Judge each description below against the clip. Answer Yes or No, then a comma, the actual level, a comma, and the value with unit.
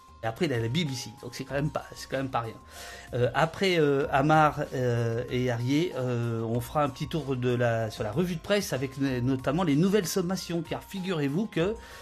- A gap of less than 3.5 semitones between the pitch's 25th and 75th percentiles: No, average, 5.1 semitones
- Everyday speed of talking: No, fast, 230 wpm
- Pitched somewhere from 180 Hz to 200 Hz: No, low, 135 Hz